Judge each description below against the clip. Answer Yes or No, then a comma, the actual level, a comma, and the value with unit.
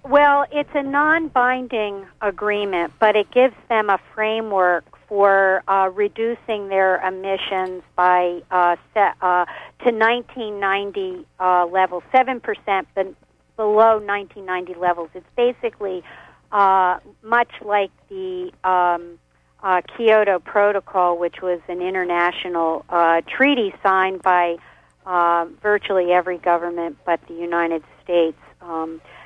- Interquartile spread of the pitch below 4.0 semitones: Yes, average, 3.6 semitones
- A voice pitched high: Yes, high, 195 Hz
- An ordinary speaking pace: No, slow, 120 wpm